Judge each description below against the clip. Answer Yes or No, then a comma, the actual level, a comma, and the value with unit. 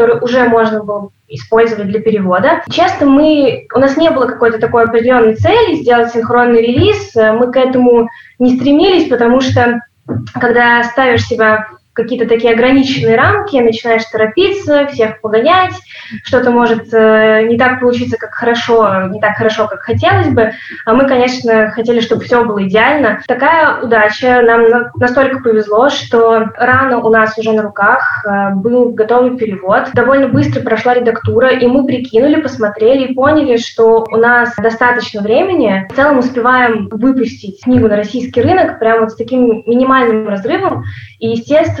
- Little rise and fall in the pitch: Yes, narrow, 2.3 semitones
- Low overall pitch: No, high, 235 Hz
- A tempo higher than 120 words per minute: Yes, average, 150 wpm